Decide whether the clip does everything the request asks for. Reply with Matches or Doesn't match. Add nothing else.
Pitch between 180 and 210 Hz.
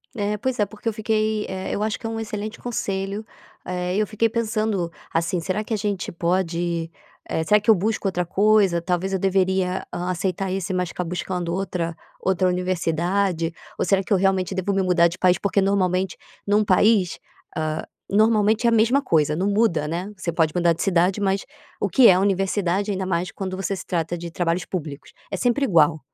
Matches